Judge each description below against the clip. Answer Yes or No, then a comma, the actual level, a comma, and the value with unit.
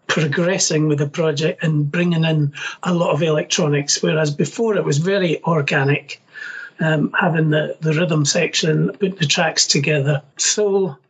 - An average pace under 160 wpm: Yes, average, 150 wpm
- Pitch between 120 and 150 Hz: No, medium, 160 Hz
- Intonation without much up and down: No, average, 3.0 semitones